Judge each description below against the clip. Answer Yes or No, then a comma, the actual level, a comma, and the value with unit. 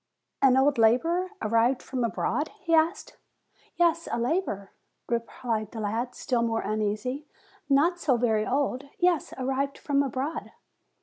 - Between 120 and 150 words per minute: Yes, slow, 135 wpm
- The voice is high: Yes, very high, 260 Hz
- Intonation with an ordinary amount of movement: Yes, average, 4.7 semitones